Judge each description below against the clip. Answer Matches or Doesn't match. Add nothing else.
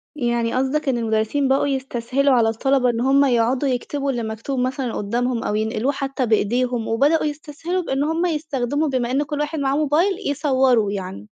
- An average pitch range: Matches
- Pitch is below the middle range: Doesn't match